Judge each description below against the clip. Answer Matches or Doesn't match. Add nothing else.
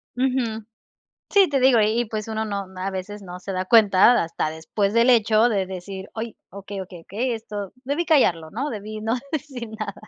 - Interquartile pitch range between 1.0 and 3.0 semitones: Doesn't match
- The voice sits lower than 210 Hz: Doesn't match